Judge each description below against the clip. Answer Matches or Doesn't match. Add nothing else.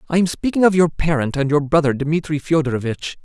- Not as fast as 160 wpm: Doesn't match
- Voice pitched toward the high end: Doesn't match